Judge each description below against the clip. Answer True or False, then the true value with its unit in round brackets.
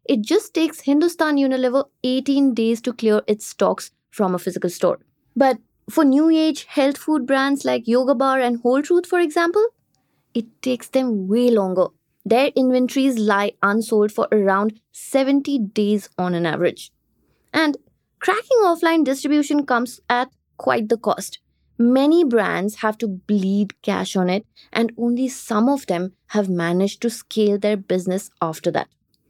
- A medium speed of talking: True (155 wpm)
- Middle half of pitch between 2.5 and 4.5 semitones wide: False (5.0 semitones)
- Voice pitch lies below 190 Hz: False (240 Hz)